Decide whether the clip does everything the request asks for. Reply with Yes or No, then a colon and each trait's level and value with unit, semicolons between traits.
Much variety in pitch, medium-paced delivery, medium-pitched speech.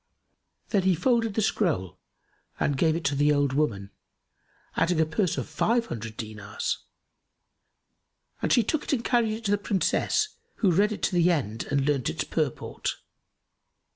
Yes: wide, 7.3 semitones; average, 170 wpm; medium, 165 Hz